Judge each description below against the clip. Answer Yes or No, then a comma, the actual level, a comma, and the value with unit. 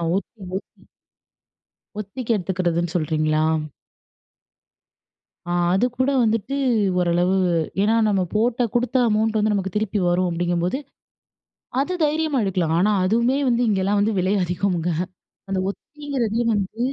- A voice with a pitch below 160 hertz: No, high, 200 Hz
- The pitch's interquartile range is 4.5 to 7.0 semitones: Yes, average, 4.8 semitones